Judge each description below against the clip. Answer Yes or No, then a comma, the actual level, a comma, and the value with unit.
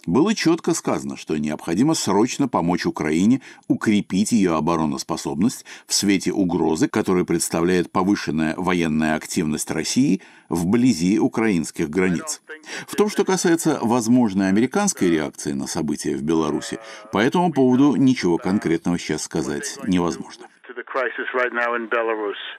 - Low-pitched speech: Yes, low, 105 Hz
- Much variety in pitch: Yes, wide, 7.0 semitones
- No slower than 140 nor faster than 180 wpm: No, slow, 110 wpm